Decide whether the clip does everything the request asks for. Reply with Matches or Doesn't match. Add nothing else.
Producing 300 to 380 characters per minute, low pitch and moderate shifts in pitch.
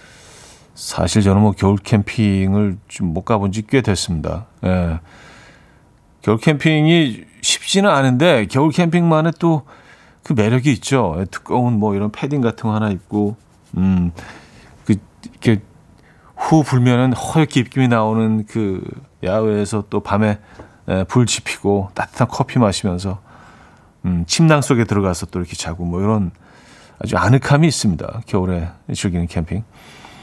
Doesn't match